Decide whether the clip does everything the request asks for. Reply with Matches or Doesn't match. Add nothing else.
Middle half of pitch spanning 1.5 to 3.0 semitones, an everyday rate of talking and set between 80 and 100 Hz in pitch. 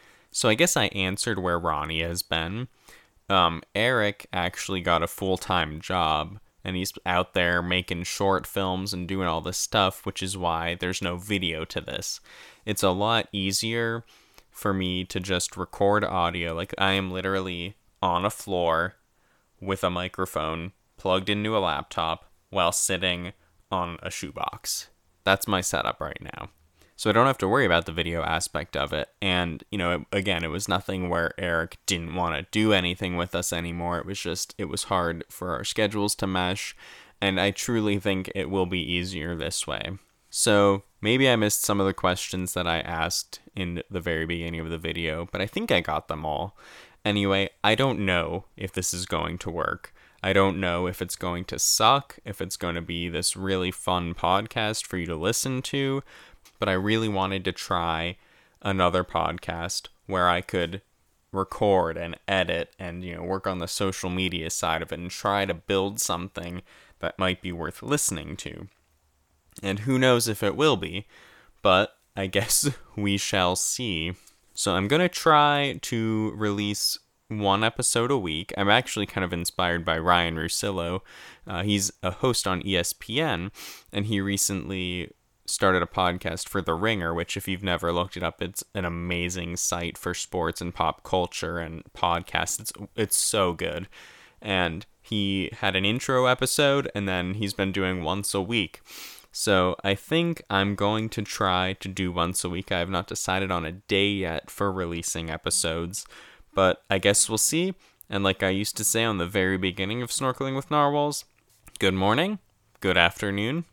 Matches